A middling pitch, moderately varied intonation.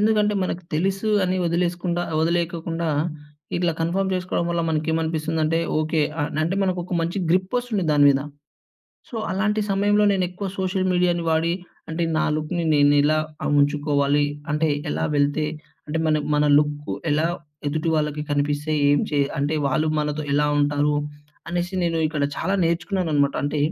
Yes: medium, 165 Hz; average, 3.3 semitones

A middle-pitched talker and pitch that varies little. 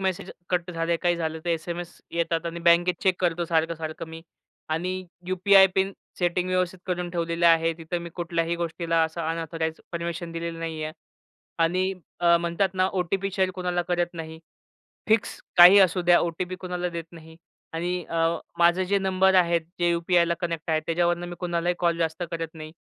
Yes: medium, 170 Hz; narrow, 1.5 semitones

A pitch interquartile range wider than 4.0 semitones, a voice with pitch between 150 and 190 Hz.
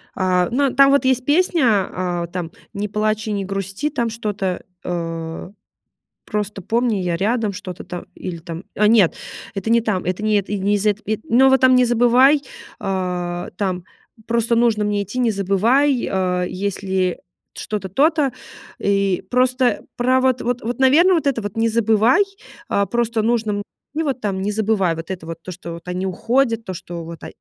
No: average, 4.6 semitones; high, 210 Hz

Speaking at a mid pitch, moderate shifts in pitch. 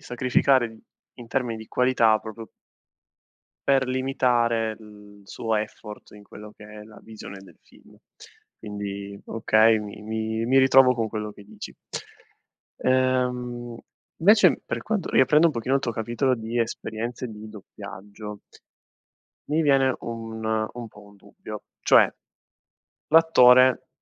No: low, 115 Hz; average, 3.1 semitones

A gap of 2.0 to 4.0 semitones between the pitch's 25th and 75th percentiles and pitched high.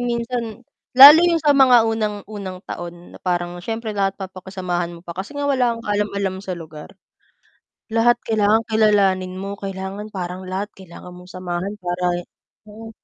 Yes: average, 3.6 semitones; high, 200 Hz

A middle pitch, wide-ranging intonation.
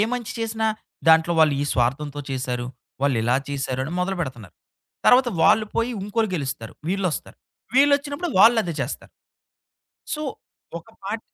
Yes: medium, 170 Hz; wide, 8.8 semitones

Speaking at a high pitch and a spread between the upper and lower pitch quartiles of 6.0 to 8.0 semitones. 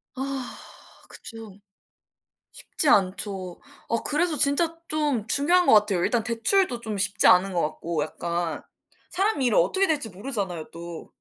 Yes: high, 225 Hz; wide, 7.7 semitones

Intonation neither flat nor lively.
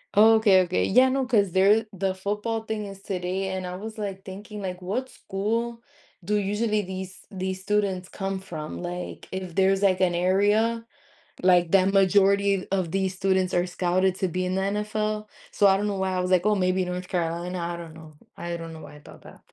No: narrow, 2.2 semitones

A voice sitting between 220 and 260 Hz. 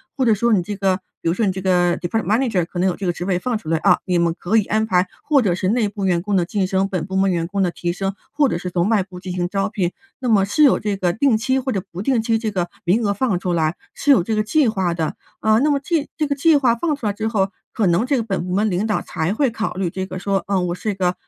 No: high, 195 Hz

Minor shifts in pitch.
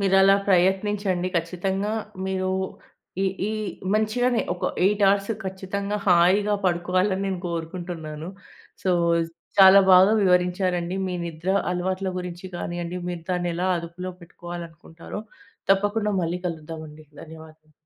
Yes: narrow, 2.2 semitones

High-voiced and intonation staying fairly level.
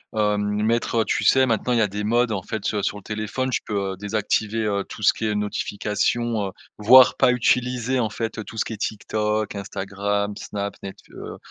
No: low, 105 Hz; narrow, 2.1 semitones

